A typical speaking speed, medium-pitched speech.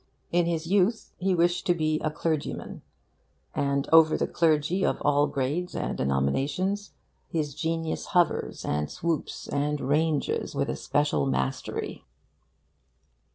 No: slow, 130 wpm; medium, 155 Hz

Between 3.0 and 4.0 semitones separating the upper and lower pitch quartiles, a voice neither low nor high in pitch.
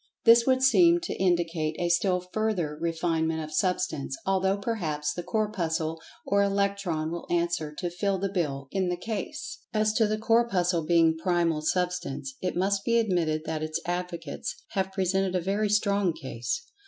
Yes: average, 3.6 semitones; medium, 180 Hz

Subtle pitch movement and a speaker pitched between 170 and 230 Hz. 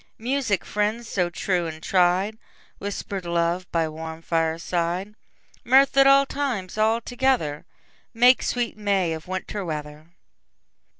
No: wide, 5.4 semitones; high, 190 Hz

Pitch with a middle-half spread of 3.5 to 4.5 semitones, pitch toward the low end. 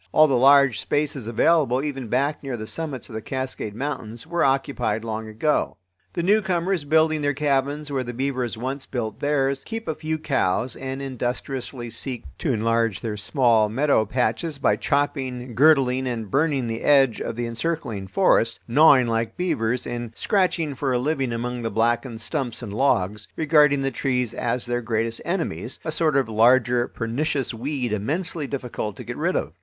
Yes: average, 4.0 semitones; low, 130 Hz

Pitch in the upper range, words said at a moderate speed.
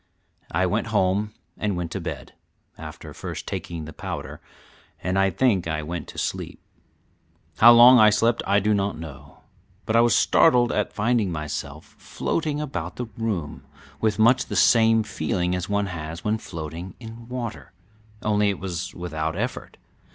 No: low, 100 Hz; average, 165 wpm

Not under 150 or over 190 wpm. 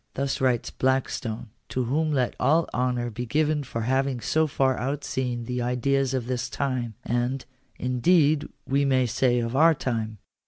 Yes: average, 160 wpm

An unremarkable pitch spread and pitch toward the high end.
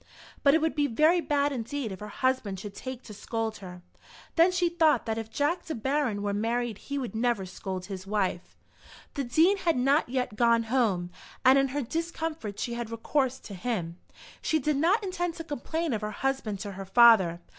No: wide, 5.9 semitones; high, 245 Hz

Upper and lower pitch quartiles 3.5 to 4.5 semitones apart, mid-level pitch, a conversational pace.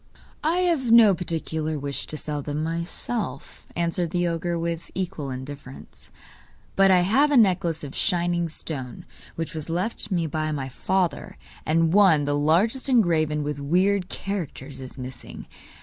Yes: average, 4.2 semitones; medium, 165 Hz; average, 150 wpm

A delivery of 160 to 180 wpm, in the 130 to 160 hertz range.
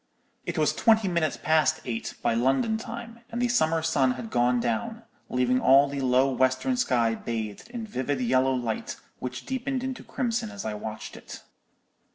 Yes: average, 175 wpm; low, 135 Hz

